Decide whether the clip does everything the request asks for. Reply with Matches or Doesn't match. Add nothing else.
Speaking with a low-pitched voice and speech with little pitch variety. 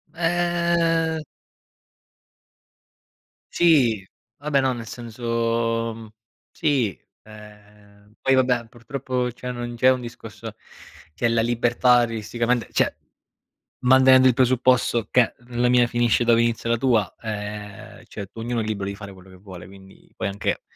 Doesn't match